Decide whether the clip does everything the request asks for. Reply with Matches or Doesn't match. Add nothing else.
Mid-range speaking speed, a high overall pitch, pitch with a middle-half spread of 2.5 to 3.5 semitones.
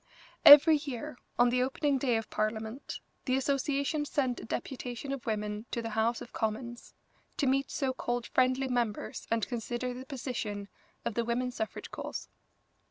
Matches